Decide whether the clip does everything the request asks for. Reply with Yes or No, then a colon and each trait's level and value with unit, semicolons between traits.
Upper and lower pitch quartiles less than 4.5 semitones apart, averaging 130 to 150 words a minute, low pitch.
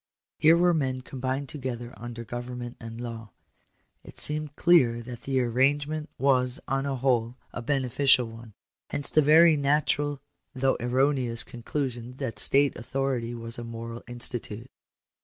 Yes: average, 2.9 semitones; average, 145 wpm; low, 130 Hz